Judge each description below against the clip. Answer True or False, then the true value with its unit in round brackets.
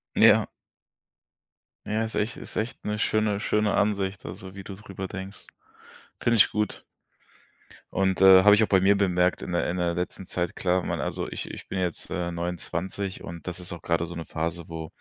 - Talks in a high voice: False (95 Hz)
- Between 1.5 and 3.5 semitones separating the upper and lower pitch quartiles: True (2.7 semitones)